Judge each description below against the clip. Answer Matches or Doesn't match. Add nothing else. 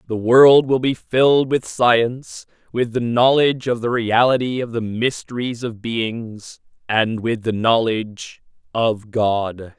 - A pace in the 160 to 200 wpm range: Doesn't match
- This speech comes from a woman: Doesn't match